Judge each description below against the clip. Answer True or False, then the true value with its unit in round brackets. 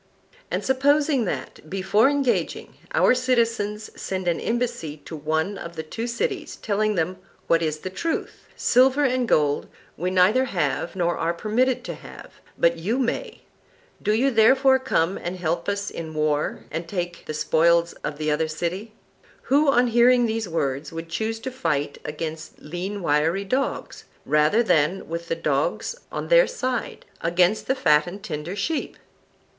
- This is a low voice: False (190 Hz)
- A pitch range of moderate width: False (6.9 semitones)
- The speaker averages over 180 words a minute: False (160 wpm)